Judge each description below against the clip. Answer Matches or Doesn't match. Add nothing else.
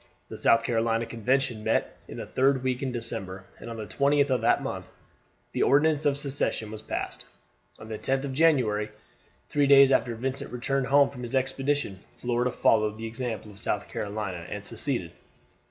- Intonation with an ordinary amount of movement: Matches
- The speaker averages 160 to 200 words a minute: Matches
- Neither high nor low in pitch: Doesn't match